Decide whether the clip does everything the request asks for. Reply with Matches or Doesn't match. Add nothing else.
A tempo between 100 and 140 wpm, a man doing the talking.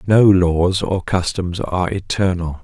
Matches